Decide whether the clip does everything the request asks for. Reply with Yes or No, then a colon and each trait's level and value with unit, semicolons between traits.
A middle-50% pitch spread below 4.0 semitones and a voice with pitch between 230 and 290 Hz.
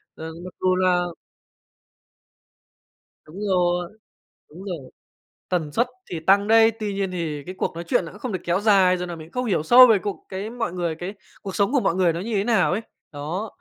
No: average, 3.2 semitones; medium, 185 Hz